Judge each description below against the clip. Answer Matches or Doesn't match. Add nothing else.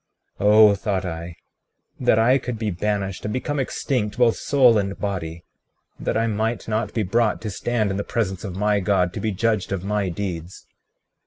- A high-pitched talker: Doesn't match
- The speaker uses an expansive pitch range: Doesn't match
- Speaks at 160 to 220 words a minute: Matches